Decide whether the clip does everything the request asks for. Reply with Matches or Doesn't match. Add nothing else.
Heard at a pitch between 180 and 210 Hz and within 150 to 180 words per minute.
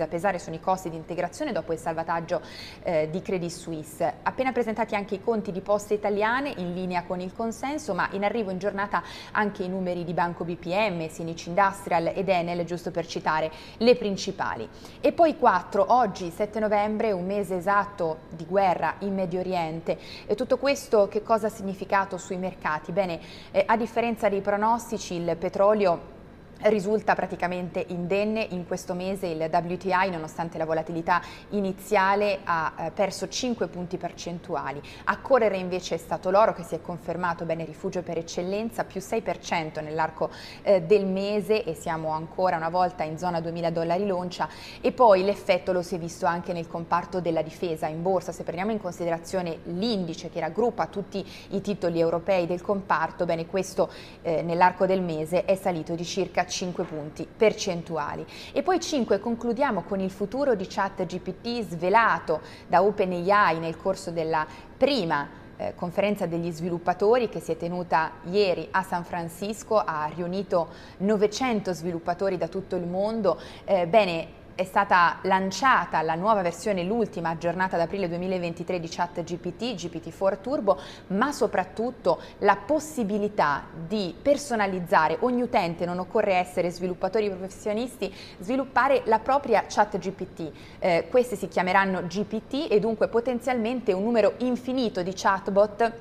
Matches